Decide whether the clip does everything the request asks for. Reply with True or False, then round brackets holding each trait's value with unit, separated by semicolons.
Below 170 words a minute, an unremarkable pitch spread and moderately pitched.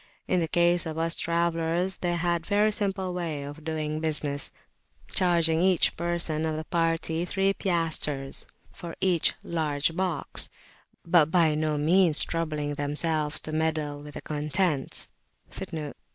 False (140 wpm; 2.2 semitones; 165 Hz)